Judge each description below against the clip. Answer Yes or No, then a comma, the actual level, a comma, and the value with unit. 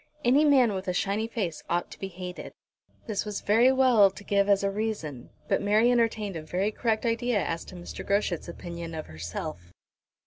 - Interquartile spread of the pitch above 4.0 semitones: Yes, average, 4.4 semitones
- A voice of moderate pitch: No, high, 200 Hz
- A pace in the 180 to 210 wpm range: Yes, average, 195 wpm